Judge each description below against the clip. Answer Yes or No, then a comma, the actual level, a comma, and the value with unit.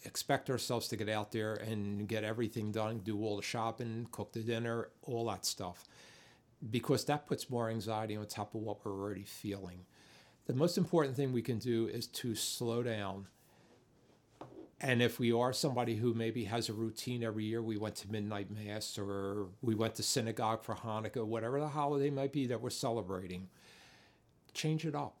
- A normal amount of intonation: No, narrow, 2.3 semitones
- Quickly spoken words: No, average, 185 wpm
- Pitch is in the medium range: No, low, 115 Hz